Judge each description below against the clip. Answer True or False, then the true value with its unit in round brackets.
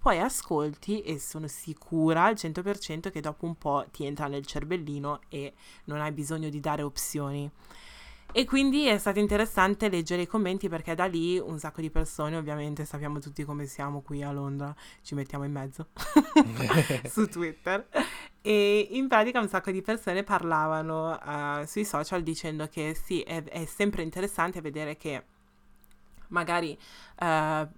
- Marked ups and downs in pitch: False (4.5 semitones)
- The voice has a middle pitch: True (160 Hz)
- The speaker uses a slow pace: False (155 wpm)